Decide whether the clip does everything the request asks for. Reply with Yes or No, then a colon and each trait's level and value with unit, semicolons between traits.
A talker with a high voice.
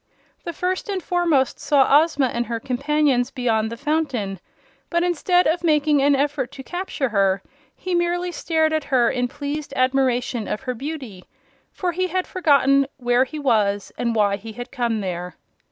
Yes: very high, 275 Hz